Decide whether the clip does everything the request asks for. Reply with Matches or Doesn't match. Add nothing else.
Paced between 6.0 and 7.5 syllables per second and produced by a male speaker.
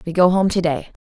Doesn't match